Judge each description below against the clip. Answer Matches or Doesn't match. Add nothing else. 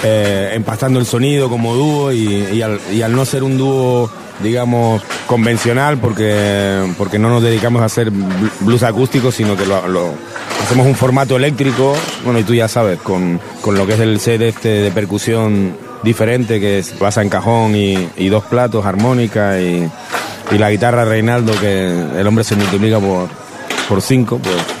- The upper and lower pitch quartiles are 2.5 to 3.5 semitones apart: Matches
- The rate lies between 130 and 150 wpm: Doesn't match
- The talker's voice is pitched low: Matches